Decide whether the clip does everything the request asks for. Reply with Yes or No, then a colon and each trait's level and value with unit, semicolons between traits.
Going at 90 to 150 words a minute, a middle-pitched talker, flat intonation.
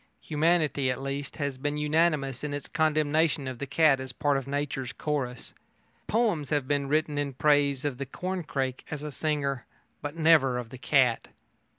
No: average, 175 wpm; medium, 145 Hz; narrow, 2.3 semitones